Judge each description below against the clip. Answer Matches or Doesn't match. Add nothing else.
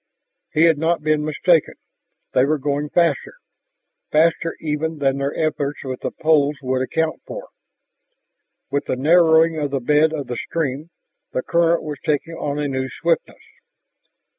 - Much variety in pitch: Doesn't match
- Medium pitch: Matches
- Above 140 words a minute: Matches